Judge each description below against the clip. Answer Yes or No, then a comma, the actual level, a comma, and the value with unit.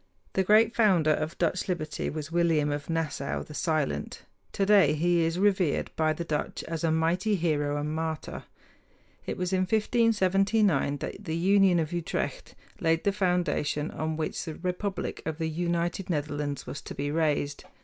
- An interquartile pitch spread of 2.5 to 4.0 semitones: Yes, average, 3.3 semitones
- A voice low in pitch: No, medium, 165 Hz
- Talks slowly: No, average, 165 wpm